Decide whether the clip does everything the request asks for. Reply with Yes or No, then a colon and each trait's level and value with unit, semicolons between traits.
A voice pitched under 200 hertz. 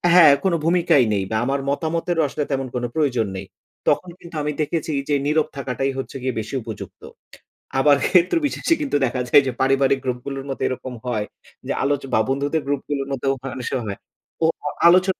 Yes: medium, 140 Hz